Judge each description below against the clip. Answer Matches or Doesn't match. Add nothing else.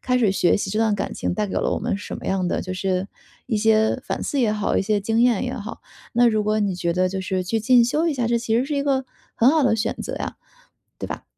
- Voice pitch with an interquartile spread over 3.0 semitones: Matches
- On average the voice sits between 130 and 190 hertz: Doesn't match